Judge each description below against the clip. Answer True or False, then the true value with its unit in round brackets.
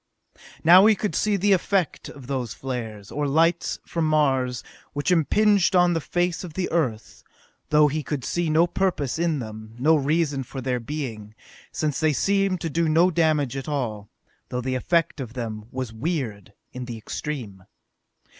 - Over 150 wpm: True (175 wpm)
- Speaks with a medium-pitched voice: True (150 Hz)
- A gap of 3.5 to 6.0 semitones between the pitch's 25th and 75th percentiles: True (5.3 semitones)